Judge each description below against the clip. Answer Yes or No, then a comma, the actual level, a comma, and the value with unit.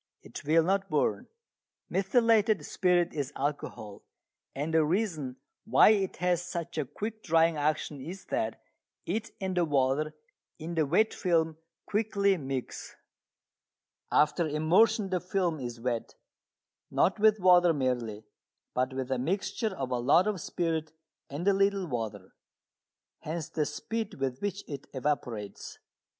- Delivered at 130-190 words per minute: Yes, average, 140 wpm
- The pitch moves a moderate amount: No, wide, 5.9 semitones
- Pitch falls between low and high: Yes, medium, 165 Hz